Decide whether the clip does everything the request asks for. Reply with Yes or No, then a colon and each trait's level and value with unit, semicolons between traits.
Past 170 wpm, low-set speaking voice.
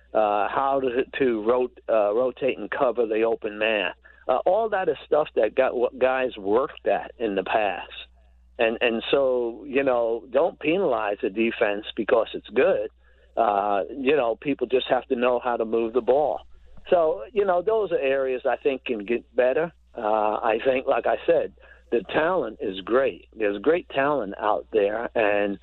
Yes: average, 185 wpm; low, 120 Hz